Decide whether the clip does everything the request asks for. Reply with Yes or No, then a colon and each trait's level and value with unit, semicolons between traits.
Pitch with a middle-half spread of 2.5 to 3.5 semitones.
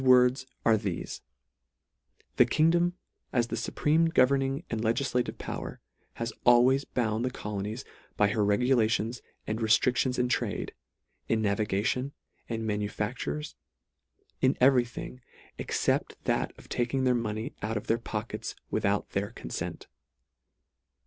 Yes: average, 3.2 semitones